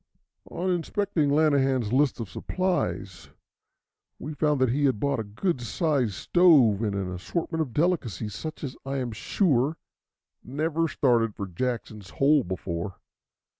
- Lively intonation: Yes, wide, 6.5 semitones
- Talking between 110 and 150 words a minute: Yes, average, 140 wpm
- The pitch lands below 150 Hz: Yes, low, 135 Hz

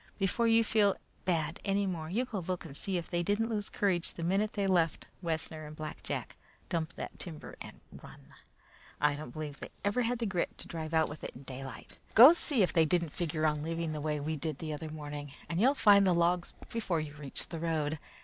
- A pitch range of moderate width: Yes, average, 4.3 semitones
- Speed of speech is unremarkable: No, fast, 225 wpm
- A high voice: No, medium, 170 Hz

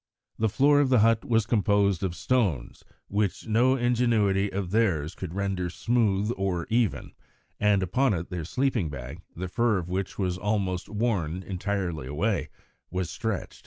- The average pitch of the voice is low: Yes, low, 100 Hz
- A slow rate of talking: No, average, 160 wpm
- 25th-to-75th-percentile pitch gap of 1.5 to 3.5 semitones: No, average, 4.0 semitones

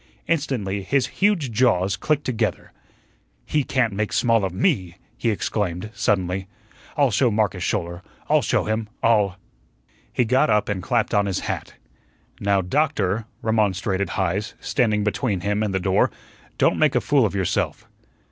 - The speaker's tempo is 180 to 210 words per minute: No, average, 160 wpm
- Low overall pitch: Yes, low, 105 Hz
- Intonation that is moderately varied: Yes, average, 3.7 semitones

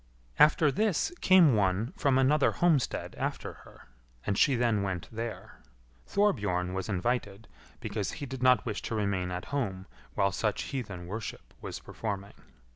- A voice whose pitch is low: Yes, low, 110 Hz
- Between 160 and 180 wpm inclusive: No, average, 150 wpm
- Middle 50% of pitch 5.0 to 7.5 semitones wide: Yes, wide, 5.5 semitones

